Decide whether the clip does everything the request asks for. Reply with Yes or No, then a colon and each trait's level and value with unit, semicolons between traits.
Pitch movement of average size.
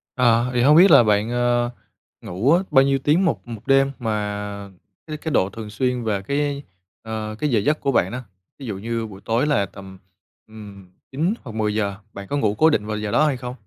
Yes: average, 4.7 semitones